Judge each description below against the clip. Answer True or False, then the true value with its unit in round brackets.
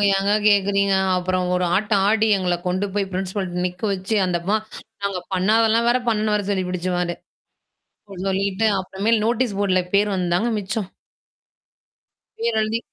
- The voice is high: True (195 Hz)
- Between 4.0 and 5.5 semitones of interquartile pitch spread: False (2.7 semitones)